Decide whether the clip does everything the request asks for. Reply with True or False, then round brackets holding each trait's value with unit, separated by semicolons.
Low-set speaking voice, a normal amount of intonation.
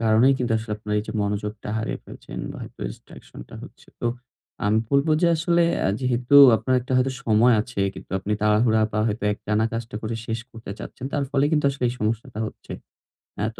True (115 Hz; 3.2 semitones)